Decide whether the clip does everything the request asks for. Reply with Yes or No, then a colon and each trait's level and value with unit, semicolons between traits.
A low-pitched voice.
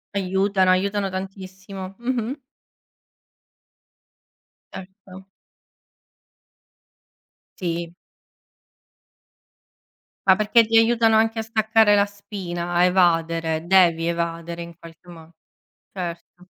No: high, 190 Hz